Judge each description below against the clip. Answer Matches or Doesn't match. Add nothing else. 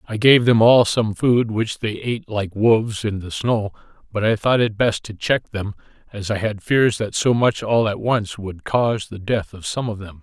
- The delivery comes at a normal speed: Doesn't match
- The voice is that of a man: Matches